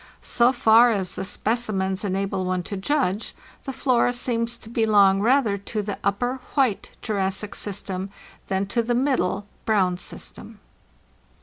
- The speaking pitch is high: Yes, high, 210 Hz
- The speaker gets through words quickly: No, average, 140 wpm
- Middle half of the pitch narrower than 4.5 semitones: Yes, average, 3.8 semitones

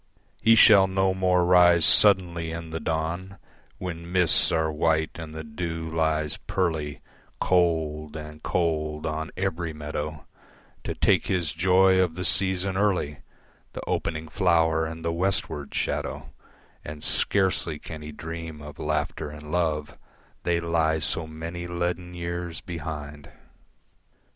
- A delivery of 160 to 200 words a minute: No, slow, 135 wpm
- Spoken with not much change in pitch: Yes, narrow, 2.3 semitones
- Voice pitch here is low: Yes, very low, 80 Hz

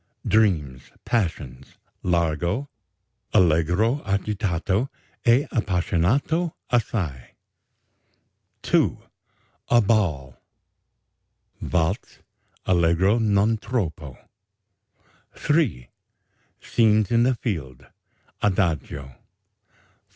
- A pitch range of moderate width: No, wide, 5.9 semitones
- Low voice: Yes, very low, 95 Hz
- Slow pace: Yes, slow, 65 wpm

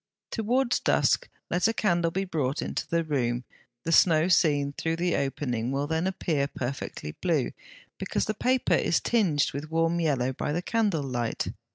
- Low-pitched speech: No, medium, 160 Hz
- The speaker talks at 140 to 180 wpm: Yes, average, 170 wpm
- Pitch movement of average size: Yes, average, 4.5 semitones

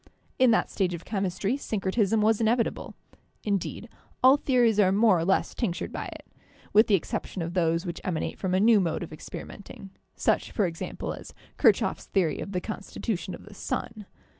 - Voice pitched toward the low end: No, high, 200 Hz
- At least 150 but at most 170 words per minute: No, average, 185 wpm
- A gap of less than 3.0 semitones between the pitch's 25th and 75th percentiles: No, average, 3.6 semitones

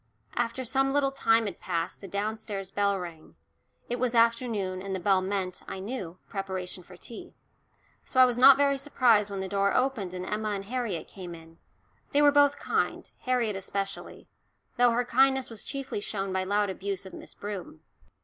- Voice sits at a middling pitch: No, high, 205 Hz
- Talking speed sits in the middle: Yes, average, 185 wpm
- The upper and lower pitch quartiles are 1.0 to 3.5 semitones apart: No, average, 4.6 semitones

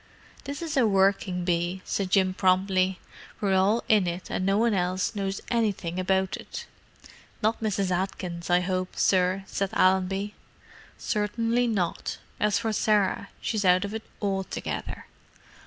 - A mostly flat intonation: Yes, narrow, 2.2 semitones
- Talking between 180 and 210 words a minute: No, average, 145 wpm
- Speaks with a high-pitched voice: Yes, high, 195 Hz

